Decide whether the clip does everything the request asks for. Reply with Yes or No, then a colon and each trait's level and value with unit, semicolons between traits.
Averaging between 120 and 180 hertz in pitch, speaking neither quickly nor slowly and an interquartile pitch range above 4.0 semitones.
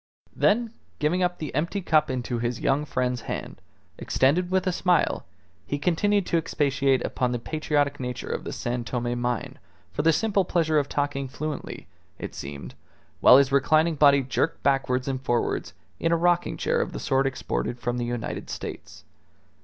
Yes: medium, 140 Hz; average, 175 wpm; average, 4.7 semitones